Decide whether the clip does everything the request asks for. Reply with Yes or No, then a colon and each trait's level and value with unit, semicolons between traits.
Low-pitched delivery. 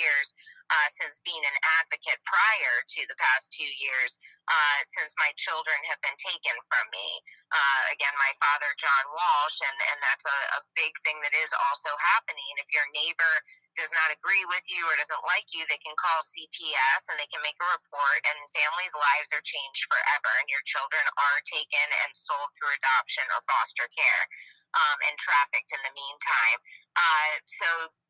No: medium, 155 Hz